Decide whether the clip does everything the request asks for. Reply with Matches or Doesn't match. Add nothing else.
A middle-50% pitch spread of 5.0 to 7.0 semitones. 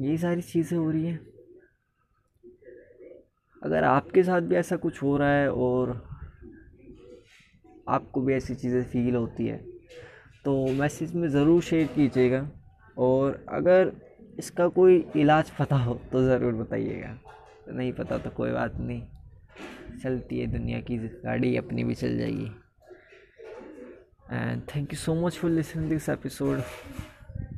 Matches